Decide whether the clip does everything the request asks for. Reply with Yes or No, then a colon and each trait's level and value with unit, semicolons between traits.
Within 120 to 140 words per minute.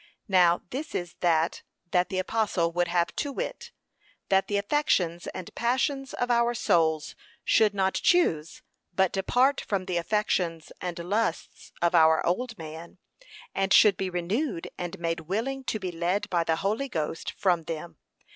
No: average, 160 wpm